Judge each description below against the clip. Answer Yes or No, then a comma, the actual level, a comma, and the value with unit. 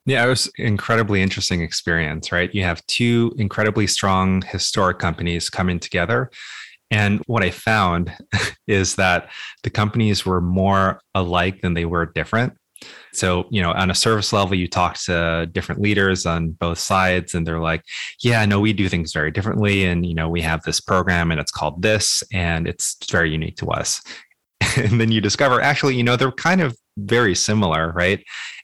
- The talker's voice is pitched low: Yes, very low, 95 Hz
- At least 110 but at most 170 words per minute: No, average, 180 wpm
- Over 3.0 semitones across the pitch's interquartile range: Yes, average, 3.7 semitones